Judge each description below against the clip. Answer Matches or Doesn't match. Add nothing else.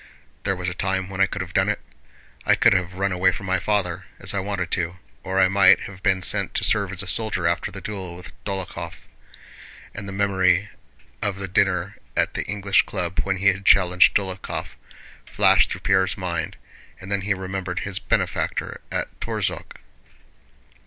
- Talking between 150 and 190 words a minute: Matches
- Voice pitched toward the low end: Matches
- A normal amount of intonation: Doesn't match